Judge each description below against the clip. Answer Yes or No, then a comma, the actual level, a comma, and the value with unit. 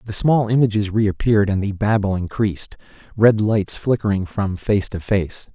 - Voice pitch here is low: Yes, low, 105 Hz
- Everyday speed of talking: Yes, average, 160 wpm